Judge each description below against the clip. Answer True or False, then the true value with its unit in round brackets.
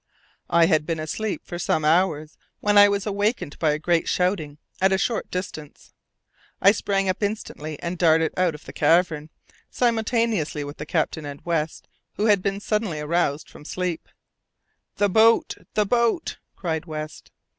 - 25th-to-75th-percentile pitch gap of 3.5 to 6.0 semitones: True (4.7 semitones)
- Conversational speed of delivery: True (165 wpm)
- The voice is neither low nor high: True (175 Hz)